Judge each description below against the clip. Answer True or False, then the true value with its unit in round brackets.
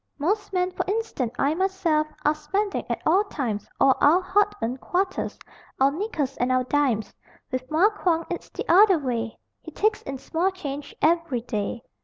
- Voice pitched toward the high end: True (310 Hz)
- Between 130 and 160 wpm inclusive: False (175 wpm)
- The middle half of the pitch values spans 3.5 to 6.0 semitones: False (6.4 semitones)